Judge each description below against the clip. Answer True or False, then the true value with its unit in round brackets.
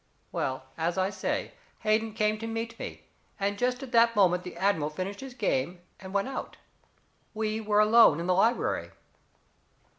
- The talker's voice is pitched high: True (210 Hz)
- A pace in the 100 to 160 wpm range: False (170 wpm)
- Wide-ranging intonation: False (3.6 semitones)